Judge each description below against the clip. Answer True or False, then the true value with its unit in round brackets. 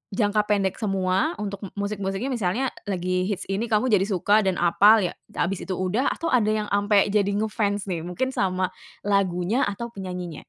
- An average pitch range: False (2.3 semitones)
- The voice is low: False (200 Hz)